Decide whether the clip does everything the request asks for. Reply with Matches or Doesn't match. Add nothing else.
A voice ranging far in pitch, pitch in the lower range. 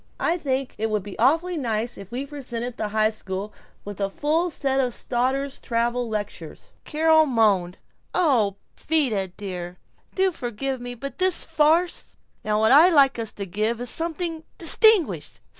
Doesn't match